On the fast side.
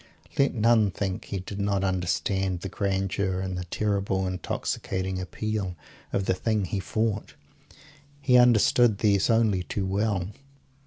No: average, 140 wpm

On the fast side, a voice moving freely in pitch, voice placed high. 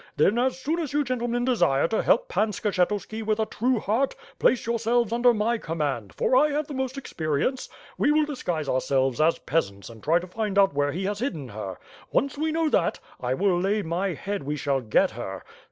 Yes: fast, 210 wpm; wide, 9.0 semitones; high, 205 Hz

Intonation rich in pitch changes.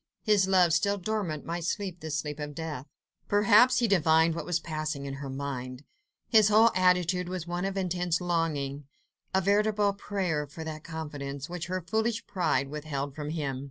No: average, 4.4 semitones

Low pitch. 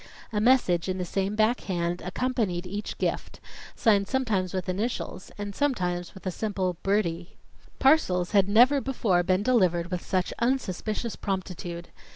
No: high, 195 Hz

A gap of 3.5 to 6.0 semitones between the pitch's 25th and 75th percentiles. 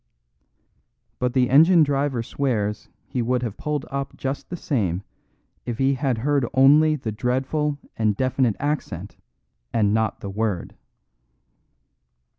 Yes: average, 4.2 semitones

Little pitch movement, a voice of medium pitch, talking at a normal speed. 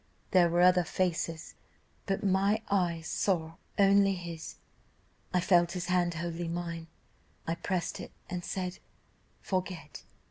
No: narrow, 1.9 semitones; medium, 175 Hz; slow, 130 wpm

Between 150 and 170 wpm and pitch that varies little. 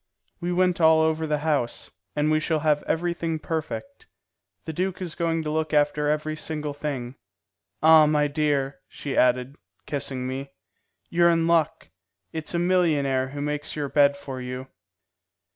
Yes: average, 160 wpm; narrow, 2.3 semitones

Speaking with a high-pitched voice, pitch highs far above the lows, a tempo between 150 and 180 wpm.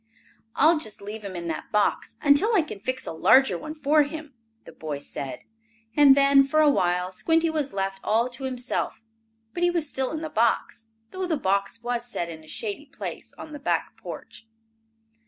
No: very high, 260 Hz; wide, 7.2 semitones; average, 195 wpm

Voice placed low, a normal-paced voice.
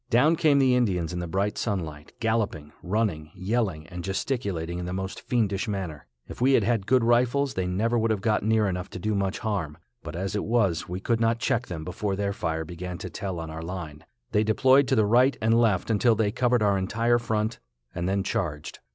No: low, 100 Hz; fast, 220 wpm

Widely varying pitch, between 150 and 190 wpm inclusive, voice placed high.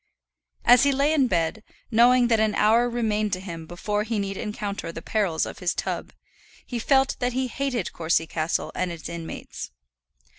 Yes: wide, 5.7 semitones; average, 180 wpm; high, 215 Hz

